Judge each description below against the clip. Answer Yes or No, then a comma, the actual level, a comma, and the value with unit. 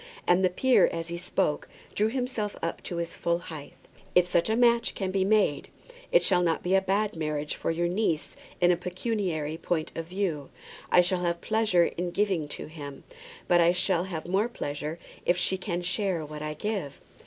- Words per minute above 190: Yes, average, 200 wpm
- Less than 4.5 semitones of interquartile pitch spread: Yes, average, 3.1 semitones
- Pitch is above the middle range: No, medium, 175 Hz